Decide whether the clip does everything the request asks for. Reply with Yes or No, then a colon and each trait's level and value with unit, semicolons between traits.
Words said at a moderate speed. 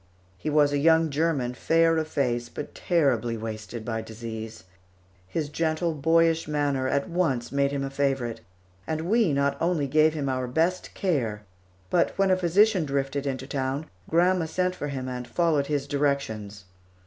Yes: average, 165 wpm